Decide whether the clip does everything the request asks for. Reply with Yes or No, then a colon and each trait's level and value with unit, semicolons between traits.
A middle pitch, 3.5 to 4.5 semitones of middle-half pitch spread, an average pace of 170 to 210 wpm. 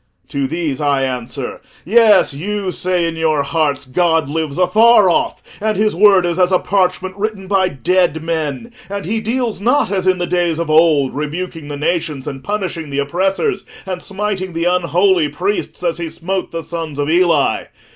Yes: medium, 175 Hz; average, 3.8 semitones; average, 180 wpm